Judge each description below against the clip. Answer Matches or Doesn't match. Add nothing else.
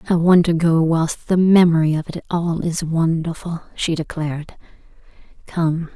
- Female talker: Matches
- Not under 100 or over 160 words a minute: Matches